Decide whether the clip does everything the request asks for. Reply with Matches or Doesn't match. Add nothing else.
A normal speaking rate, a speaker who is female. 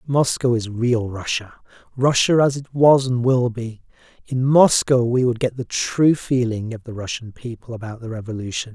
Doesn't match